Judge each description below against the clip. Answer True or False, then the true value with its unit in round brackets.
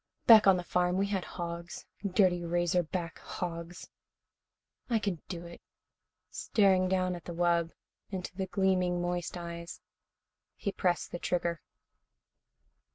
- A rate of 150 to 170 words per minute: False (135 wpm)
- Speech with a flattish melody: True (1.6 semitones)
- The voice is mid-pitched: True (180 Hz)